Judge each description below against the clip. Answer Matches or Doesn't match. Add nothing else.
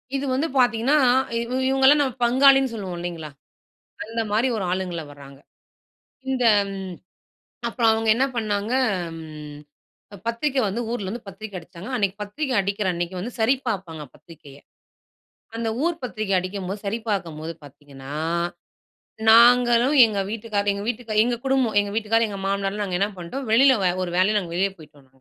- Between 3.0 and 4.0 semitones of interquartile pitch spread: Doesn't match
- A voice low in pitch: Doesn't match